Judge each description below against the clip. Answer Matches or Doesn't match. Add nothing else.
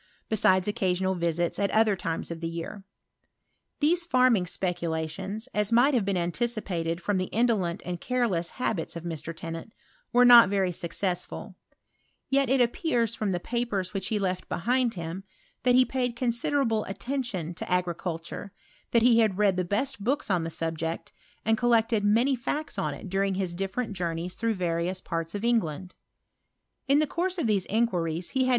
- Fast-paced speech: Doesn't match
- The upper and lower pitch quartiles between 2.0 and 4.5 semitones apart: Doesn't match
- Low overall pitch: Doesn't match